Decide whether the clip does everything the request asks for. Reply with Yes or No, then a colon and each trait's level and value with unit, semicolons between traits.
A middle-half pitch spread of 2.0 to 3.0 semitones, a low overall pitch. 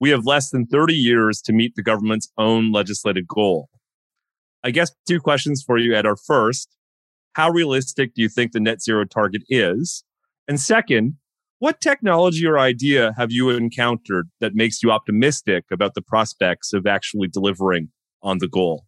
No: average, 5.3 semitones; low, 120 Hz